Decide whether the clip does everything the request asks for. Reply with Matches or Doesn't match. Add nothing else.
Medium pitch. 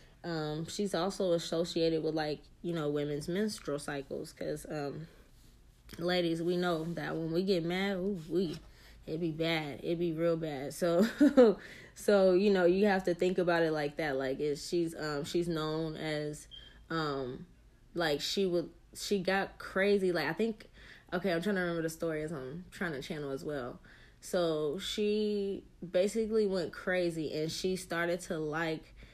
Matches